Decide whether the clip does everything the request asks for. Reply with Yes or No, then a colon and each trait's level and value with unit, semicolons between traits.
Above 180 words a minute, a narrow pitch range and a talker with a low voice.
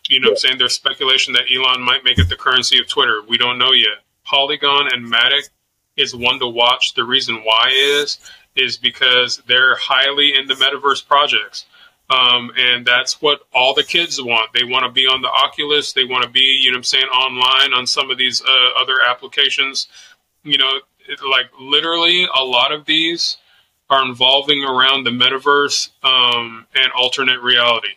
Yes: average, 190 wpm; narrow, 2.3 semitones; low, 130 Hz